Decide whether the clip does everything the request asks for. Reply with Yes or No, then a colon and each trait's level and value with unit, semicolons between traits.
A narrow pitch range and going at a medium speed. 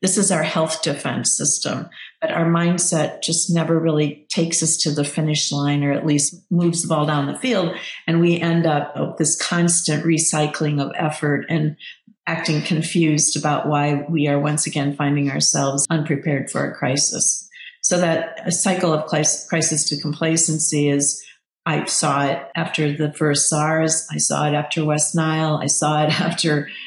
Yes: narrow, 1.9 semitones; average, 170 wpm